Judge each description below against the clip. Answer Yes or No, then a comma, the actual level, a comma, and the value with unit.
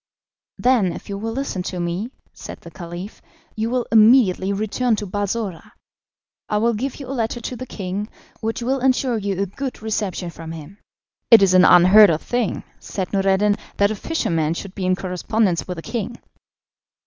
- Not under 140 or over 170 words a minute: No, average, 185 wpm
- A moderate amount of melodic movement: Yes, average, 4.0 semitones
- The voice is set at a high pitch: Yes, high, 205 Hz